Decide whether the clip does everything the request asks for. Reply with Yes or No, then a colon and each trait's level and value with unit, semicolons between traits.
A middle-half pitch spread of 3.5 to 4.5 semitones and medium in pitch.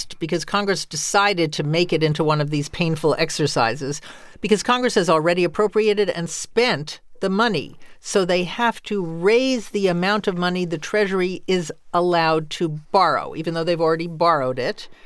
Yes: average, 4.2 semitones; medium, 175 Hz